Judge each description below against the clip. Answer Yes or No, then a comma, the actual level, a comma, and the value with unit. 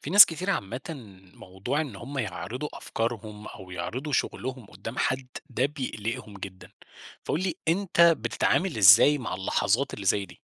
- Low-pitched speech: Yes, low, 125 Hz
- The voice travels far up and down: Yes, wide, 6.7 semitones